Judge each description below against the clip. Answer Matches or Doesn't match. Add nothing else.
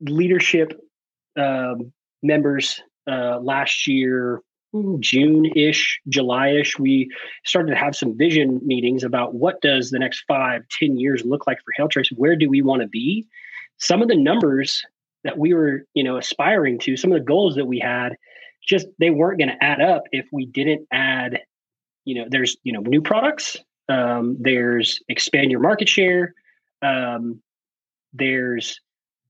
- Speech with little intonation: Doesn't match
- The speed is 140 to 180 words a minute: Matches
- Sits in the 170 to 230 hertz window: Doesn't match